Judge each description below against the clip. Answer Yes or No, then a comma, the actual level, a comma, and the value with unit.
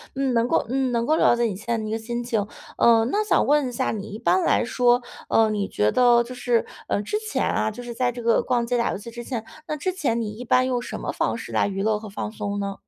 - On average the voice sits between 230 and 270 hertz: Yes, high, 235 Hz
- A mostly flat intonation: Yes, narrow, 2.3 semitones